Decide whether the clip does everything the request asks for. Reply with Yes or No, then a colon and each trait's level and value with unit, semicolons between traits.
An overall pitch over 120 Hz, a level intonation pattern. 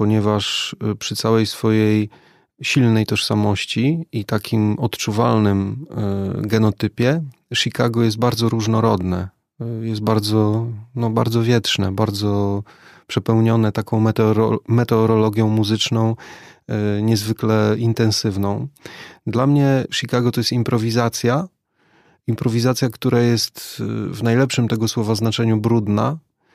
No: low, 115 Hz; narrow, 1.8 semitones